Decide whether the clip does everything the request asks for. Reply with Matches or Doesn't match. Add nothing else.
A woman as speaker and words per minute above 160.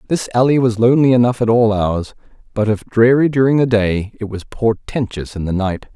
Doesn't match